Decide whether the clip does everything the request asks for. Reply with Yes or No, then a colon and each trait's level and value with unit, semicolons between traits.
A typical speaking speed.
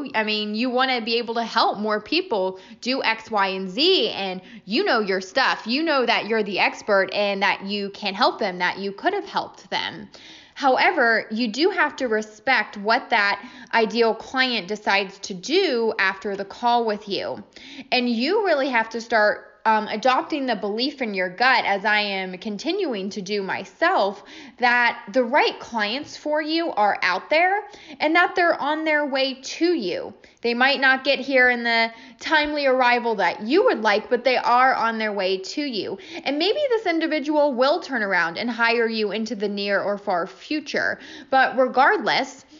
Yes: average, 185 wpm